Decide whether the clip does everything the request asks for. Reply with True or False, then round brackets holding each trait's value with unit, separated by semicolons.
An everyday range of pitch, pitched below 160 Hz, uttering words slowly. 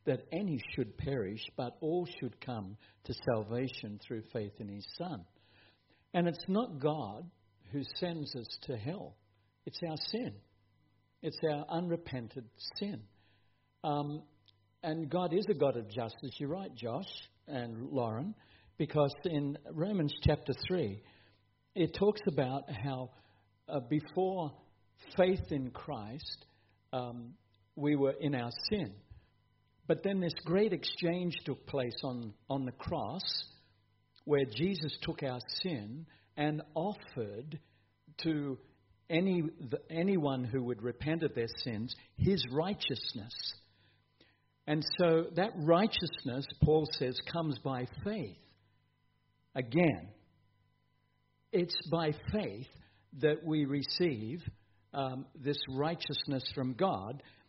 False (6.2 semitones; 135 Hz; 120 wpm)